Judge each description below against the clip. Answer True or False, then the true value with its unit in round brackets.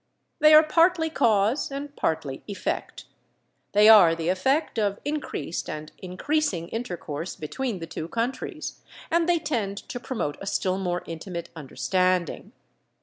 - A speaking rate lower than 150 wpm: True (140 wpm)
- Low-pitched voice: False (200 Hz)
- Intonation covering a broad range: True (8.4 semitones)